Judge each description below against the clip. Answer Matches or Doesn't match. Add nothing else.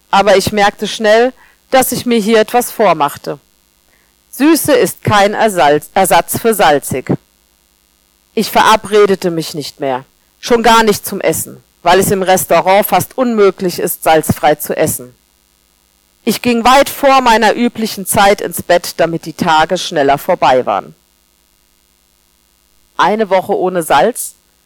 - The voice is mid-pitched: Matches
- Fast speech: Doesn't match